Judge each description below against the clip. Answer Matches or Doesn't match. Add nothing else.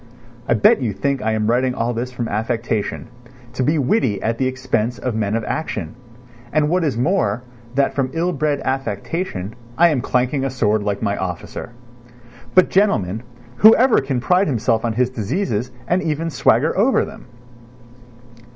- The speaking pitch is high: Doesn't match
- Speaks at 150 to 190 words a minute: Matches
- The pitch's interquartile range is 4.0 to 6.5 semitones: Matches